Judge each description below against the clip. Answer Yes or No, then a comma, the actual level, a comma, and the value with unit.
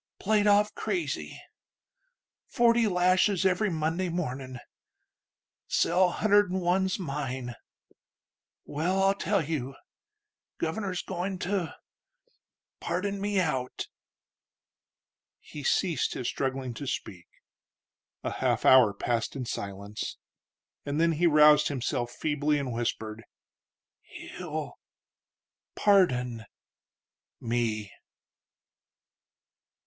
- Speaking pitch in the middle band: Yes, medium, 155 Hz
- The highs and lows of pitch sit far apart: Yes, wide, 6.9 semitones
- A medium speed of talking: No, slow, 90 wpm